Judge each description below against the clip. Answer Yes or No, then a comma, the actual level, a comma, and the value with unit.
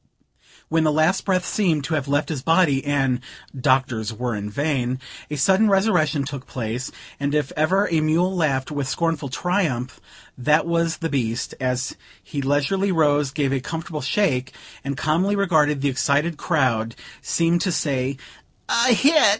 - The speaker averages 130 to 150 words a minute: No, average, 160 wpm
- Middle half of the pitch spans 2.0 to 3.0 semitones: No, average, 4.2 semitones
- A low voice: No, medium, 150 Hz